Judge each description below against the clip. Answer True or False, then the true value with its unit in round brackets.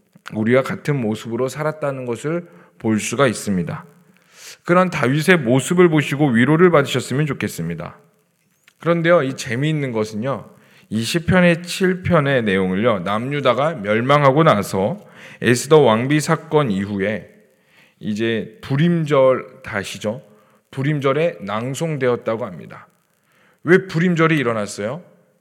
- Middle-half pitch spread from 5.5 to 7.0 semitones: True (6.2 semitones)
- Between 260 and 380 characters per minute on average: True (280 characters per minute)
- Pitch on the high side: False (140 Hz)